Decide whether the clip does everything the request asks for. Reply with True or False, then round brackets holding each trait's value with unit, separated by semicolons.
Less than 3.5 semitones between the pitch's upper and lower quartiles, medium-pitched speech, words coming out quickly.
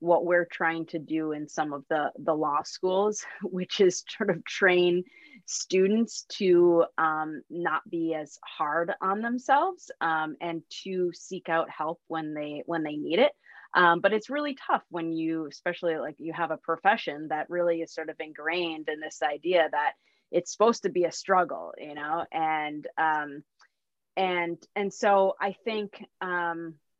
False (3.0 semitones; 170 Hz; 170 wpm)